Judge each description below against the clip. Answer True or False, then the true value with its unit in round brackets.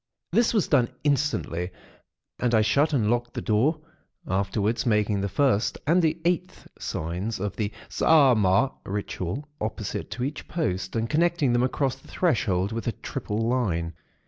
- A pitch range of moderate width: False (6.2 semitones)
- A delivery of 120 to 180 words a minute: True (155 wpm)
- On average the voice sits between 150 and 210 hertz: False (115 Hz)